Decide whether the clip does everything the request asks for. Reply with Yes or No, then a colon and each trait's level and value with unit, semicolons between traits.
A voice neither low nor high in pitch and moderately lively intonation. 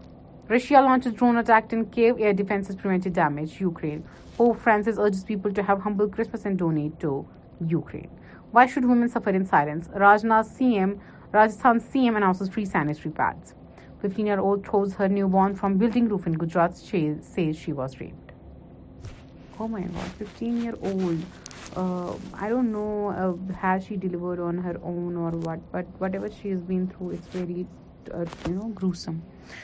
No: high, 195 Hz; average, 3.6 semitones